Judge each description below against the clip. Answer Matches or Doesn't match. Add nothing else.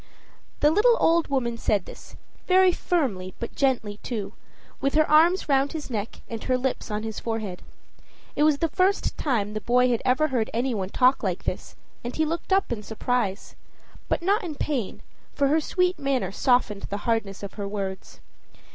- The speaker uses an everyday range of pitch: Doesn't match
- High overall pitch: Matches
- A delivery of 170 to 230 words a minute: Matches